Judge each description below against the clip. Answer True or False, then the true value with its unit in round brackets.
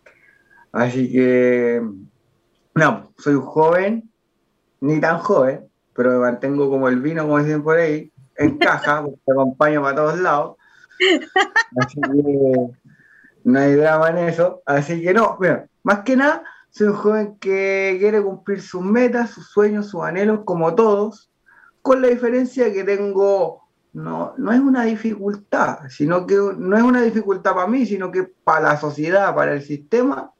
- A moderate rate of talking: True (160 wpm)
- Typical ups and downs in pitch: False (6.7 semitones)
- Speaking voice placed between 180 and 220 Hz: True (185 Hz)